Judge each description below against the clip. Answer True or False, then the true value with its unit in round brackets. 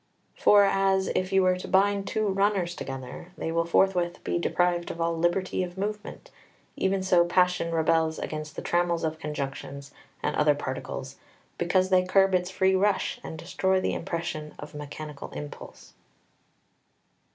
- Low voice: False (175 Hz)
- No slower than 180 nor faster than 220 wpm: False (160 wpm)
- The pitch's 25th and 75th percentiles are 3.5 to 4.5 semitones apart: False (2.7 semitones)